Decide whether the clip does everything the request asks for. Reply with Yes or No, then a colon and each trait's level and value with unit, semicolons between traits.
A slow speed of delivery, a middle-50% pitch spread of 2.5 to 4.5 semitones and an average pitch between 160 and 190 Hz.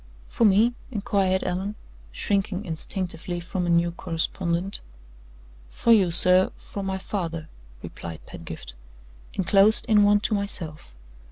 Yes: slow, 120 wpm; average, 3.1 semitones; medium, 185 Hz